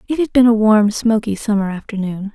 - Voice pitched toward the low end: No, high, 215 Hz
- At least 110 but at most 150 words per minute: No, fast, 205 wpm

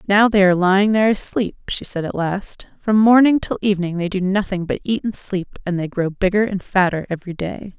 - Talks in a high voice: Yes, high, 195 Hz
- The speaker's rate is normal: No, fast, 225 wpm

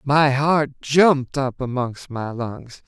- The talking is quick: No, average, 145 wpm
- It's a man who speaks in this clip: Yes, male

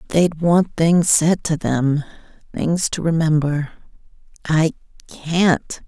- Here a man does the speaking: No, female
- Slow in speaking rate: Yes, slow, 90 wpm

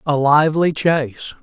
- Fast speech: No, slow, 125 wpm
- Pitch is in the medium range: Yes, medium, 150 Hz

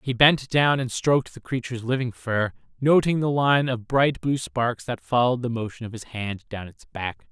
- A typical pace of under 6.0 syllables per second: Yes, 5.0 syllables/s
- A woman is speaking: No, male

